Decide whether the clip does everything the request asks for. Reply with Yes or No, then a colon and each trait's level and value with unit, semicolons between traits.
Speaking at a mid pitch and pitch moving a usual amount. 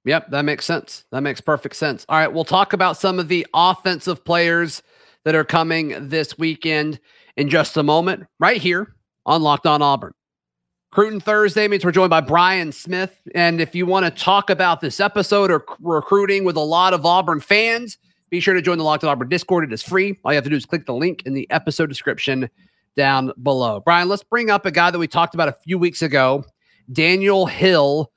Yes: medium, 170 Hz; average, 3.6 semitones